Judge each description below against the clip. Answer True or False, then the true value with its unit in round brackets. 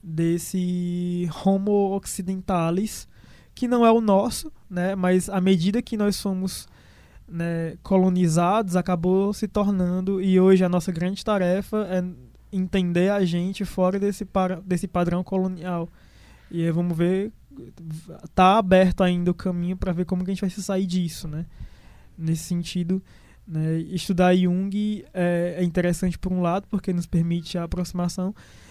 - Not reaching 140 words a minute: False (150 wpm)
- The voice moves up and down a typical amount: False (1.7 semitones)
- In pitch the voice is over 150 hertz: True (185 Hz)